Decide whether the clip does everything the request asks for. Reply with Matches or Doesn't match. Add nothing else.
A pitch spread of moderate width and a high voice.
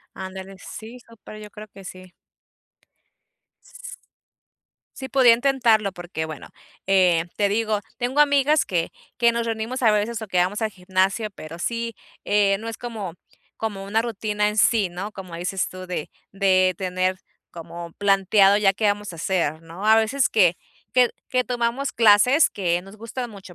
Matches